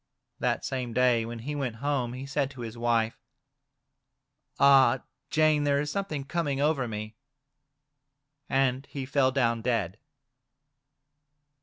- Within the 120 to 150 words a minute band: Yes, slow, 135 wpm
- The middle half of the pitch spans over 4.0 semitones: No, average, 3.2 semitones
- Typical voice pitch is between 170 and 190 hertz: No, low, 130 Hz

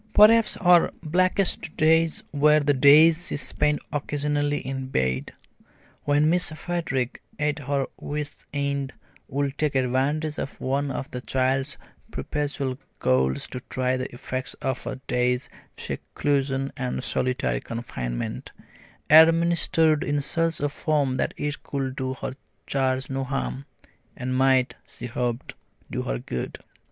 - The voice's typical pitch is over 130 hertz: Yes, medium, 140 Hz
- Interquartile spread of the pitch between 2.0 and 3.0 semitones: Yes, average, 2.7 semitones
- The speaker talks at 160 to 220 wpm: No, slow, 135 wpm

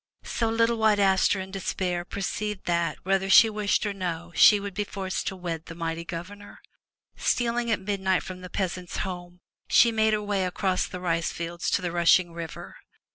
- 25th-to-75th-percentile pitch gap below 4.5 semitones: Yes, average, 2.8 semitones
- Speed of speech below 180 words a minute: No, average, 185 wpm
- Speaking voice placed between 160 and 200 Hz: Yes, high, 190 Hz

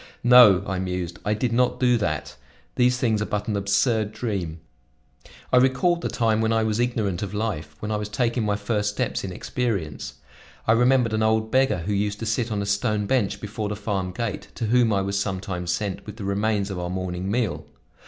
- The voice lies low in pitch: Yes, low, 105 Hz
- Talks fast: Yes, fast, 210 wpm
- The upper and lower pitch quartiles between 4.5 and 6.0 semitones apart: No, average, 2.8 semitones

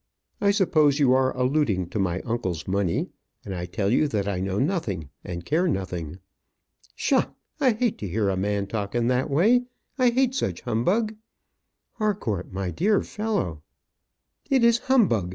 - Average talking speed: Yes, average, 170 wpm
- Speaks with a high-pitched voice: No, low, 120 Hz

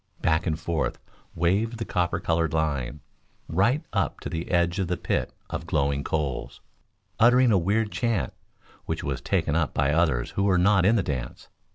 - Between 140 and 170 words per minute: No, average, 180 wpm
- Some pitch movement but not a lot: Yes, average, 4.7 semitones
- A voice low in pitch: Yes, very low, 85 Hz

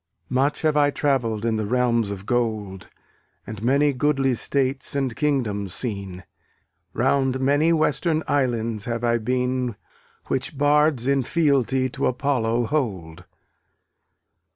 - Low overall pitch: Yes, low, 125 Hz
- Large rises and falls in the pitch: No, average, 3.9 semitones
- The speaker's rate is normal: No, slow, 125 wpm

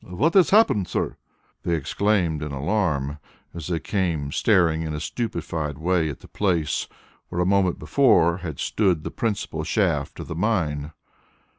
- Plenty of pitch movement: No, average, 4.5 semitones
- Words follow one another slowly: No, average, 160 wpm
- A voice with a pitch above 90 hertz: No, very low, 85 Hz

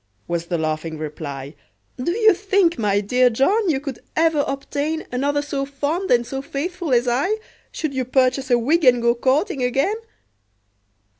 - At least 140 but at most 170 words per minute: Yes, average, 165 wpm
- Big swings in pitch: No, average, 5.0 semitones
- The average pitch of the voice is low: No, very high, 270 Hz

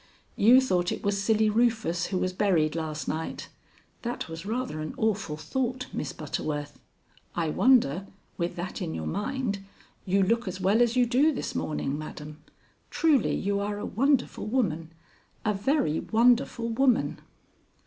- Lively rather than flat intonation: Yes, wide, 6.7 semitones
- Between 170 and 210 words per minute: No, average, 155 wpm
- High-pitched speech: Yes, high, 200 Hz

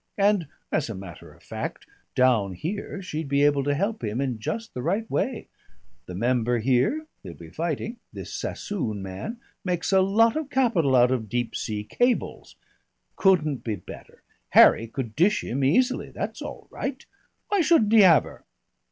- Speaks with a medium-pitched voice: Yes, medium, 150 Hz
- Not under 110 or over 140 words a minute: No, average, 170 wpm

